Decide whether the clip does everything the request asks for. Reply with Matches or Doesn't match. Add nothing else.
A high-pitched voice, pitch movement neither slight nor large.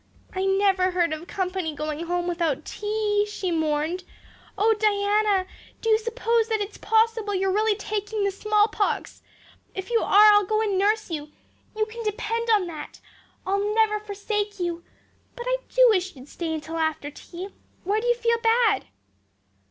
Matches